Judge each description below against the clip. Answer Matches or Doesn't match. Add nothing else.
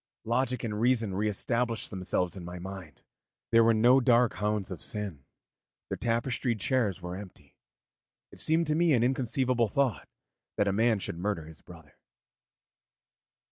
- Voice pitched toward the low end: Matches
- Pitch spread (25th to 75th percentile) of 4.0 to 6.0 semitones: Matches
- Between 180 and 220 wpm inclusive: Doesn't match